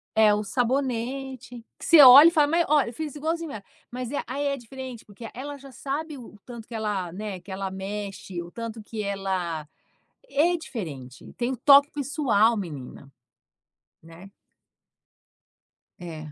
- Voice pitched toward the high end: Yes, high, 230 Hz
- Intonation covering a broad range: Yes, wide, 6.1 semitones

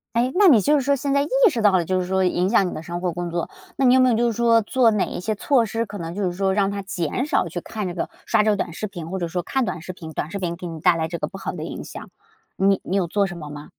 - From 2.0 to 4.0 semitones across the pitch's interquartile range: No, average, 4.6 semitones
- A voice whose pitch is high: Yes, high, 195 Hz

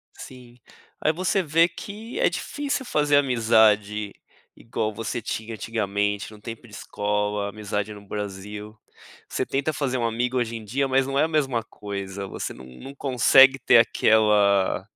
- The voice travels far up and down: No, average, 4.6 semitones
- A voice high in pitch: No, low, 115 Hz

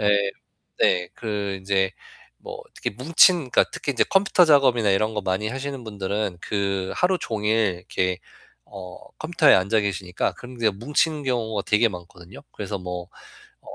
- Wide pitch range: No, average, 5.0 semitones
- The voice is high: No, low, 105 Hz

